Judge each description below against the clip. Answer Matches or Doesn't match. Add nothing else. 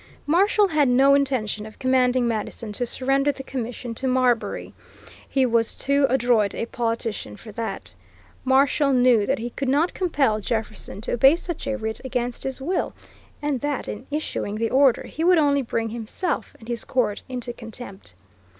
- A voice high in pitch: Matches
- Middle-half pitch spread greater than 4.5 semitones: Doesn't match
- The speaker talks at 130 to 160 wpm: Doesn't match